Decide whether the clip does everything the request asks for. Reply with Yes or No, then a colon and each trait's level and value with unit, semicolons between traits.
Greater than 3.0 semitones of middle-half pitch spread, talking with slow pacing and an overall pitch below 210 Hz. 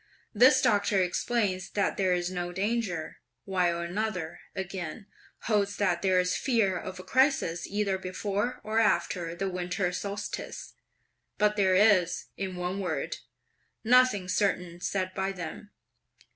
No: narrow, 2.6 semitones; slow, 130 wpm; high, 190 Hz